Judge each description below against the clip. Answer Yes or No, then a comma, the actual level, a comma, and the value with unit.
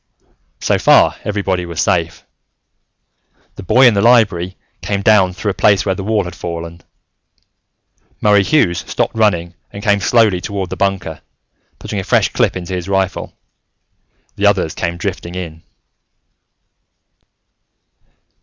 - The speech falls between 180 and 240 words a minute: No, slow, 135 wpm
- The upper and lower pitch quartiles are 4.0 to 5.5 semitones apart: No, average, 2.8 semitones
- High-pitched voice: No, very low, 95 Hz